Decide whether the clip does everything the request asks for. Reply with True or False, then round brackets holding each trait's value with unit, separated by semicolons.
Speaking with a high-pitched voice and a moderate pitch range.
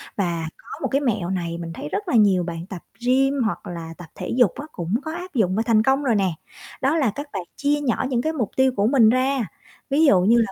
False (230 Hz; 6.8 semitones)